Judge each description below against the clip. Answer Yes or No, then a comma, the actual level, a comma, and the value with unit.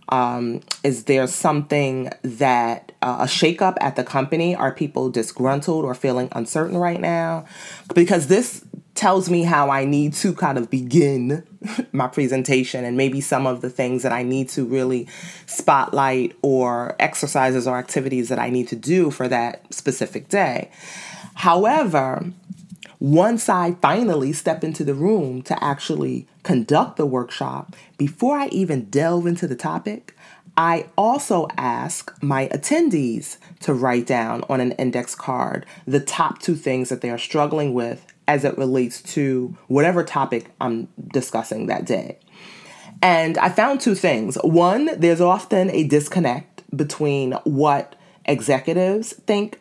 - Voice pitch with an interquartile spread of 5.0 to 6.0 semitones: Yes, average, 5.3 semitones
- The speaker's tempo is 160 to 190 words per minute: No, average, 150 wpm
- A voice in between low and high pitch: Yes, medium, 145 Hz